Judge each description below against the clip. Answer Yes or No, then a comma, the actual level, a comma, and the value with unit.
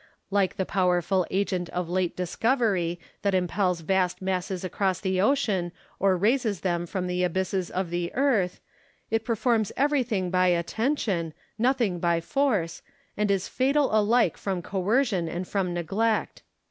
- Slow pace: No, average, 145 wpm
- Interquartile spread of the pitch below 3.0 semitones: No, average, 3.6 semitones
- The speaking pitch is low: No, high, 190 Hz